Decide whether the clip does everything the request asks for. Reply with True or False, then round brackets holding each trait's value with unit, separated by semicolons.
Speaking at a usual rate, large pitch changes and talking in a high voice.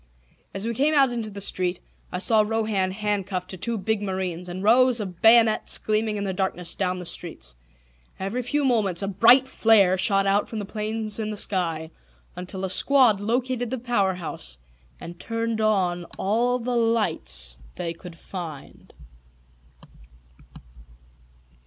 False (155 wpm; 3.9 semitones; 205 Hz)